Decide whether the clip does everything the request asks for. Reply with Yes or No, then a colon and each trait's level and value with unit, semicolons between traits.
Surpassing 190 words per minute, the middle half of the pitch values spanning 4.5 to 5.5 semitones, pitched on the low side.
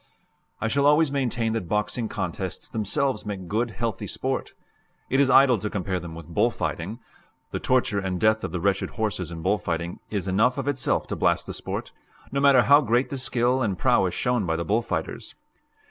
Yes: average, 200 wpm; average, 5.2 semitones; low, 110 Hz